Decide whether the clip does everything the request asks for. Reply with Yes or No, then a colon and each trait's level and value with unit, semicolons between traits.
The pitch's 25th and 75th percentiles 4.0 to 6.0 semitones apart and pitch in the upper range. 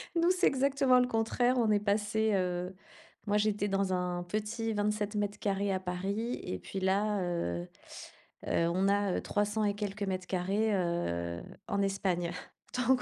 No: average, 2.8 semitones; high, 205 Hz